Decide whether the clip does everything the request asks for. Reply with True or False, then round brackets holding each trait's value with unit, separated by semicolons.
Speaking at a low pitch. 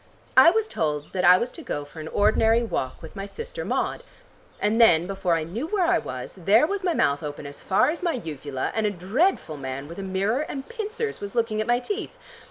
False (205 Hz)